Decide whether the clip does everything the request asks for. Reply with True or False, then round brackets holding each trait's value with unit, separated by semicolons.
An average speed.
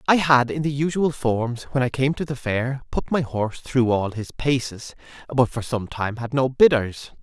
False (215 wpm)